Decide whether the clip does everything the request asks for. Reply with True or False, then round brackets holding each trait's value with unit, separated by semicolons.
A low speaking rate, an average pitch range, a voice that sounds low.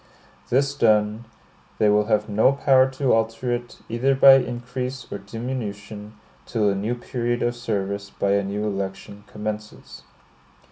False (145 wpm; 3.3 semitones; 115 Hz)